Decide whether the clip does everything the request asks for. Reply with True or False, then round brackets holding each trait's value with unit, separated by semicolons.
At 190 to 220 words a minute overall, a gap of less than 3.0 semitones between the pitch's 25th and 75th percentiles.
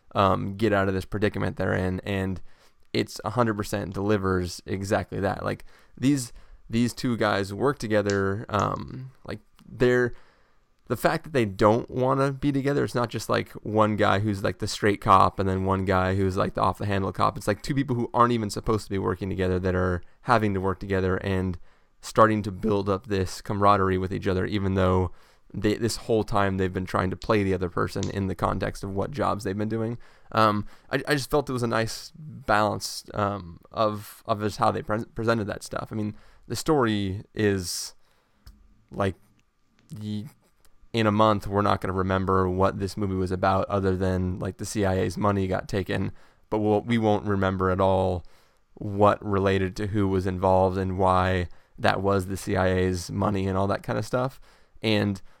True (195 wpm; 2.6 semitones)